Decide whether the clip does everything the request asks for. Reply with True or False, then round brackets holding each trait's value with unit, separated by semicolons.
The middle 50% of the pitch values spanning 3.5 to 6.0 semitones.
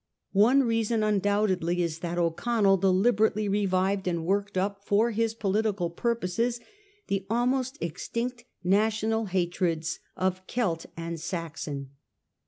True (4.0 semitones)